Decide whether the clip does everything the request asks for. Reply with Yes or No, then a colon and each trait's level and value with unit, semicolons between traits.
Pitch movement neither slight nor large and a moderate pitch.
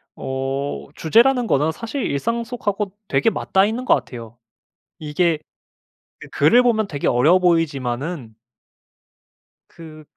No: wide, 8.1 semitones; medium, 165 Hz